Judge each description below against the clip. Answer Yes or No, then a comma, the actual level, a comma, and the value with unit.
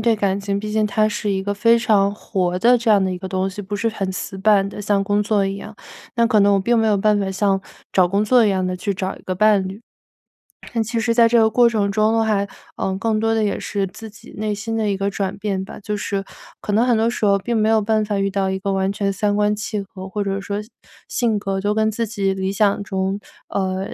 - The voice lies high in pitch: Yes, high, 205 Hz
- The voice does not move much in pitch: Yes, narrow, 2.0 semitones